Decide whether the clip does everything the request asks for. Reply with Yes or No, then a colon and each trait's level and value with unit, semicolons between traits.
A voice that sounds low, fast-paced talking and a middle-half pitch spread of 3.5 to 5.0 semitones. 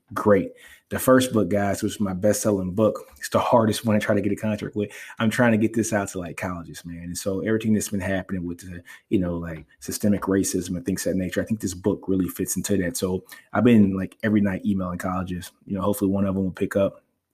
No: low, 100 Hz; fast, 255 wpm; narrow, 2.5 semitones